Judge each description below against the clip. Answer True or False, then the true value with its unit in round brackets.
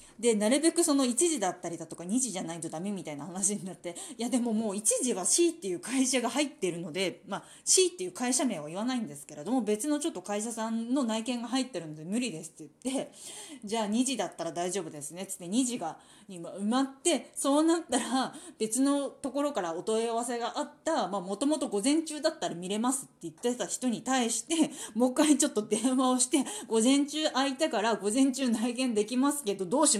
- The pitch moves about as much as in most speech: False (5.8 semitones)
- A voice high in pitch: True (245 Hz)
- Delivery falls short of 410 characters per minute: False (430 characters per minute)